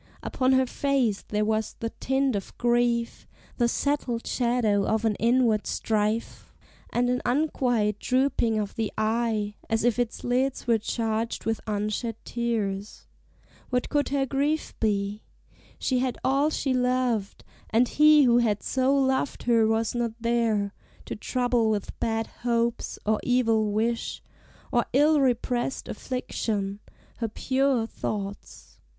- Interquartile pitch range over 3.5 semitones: No, average, 2.8 semitones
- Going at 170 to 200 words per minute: No, average, 140 wpm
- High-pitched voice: Yes, high, 235 Hz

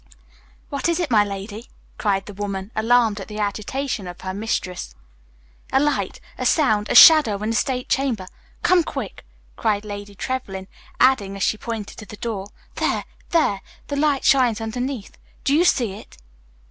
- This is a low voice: No, high, 220 Hz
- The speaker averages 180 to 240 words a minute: No, average, 170 wpm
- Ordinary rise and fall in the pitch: Yes, average, 4.5 semitones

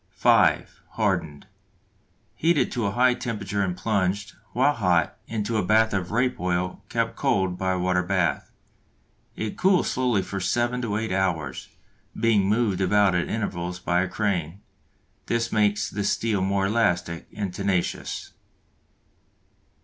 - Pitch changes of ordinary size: Yes, average, 3.7 semitones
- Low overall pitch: Yes, low, 100 Hz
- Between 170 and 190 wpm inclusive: No, average, 140 wpm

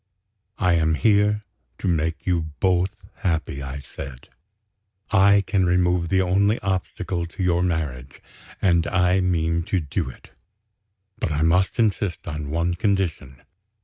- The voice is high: No, very low, 90 Hz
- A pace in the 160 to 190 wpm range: No, average, 140 wpm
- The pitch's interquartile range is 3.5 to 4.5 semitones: No, average, 2.9 semitones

